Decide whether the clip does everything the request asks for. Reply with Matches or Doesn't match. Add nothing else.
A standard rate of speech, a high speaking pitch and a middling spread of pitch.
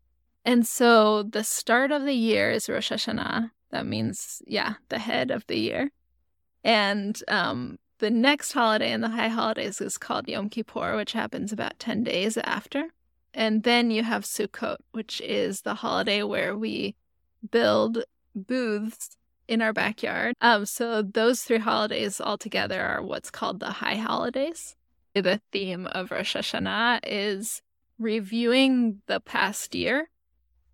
Doesn't match